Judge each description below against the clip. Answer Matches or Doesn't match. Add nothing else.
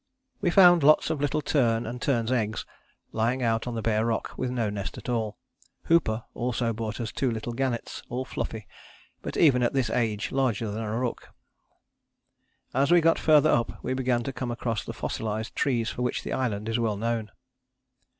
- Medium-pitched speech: Doesn't match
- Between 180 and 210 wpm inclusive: Matches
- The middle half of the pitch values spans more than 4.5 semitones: Doesn't match